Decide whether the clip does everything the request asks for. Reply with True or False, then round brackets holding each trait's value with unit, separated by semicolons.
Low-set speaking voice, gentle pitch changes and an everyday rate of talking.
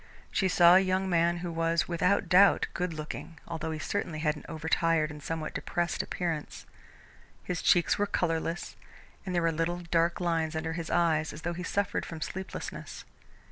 False (170 Hz; 1.6 semitones; 180 wpm)